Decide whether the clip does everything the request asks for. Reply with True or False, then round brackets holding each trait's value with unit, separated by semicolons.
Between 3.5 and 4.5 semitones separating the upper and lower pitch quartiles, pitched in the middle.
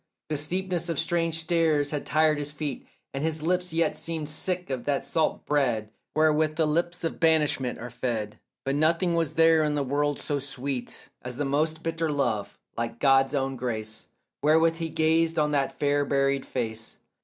False (3.0 semitones; 150 Hz)